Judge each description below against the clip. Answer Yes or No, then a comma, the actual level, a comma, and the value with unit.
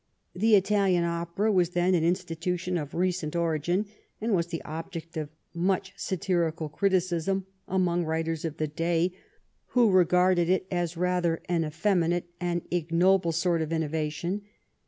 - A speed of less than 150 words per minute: Yes, average, 140 wpm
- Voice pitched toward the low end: No, medium, 175 Hz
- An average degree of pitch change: No, narrow, 2.1 semitones